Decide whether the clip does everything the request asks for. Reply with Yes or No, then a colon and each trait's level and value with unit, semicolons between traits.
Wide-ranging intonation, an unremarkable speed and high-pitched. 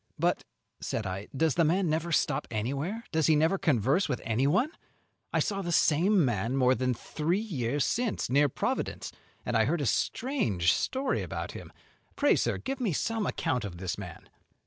No: wide, 7.9 semitones; average, 180 wpm; medium, 150 Hz